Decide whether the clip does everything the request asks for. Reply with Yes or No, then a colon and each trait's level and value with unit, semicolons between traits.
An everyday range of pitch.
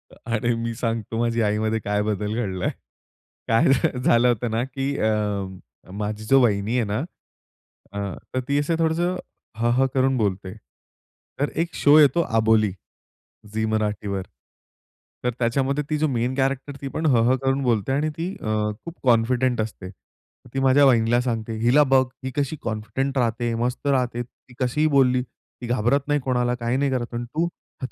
Yes: average, 3.5 semitones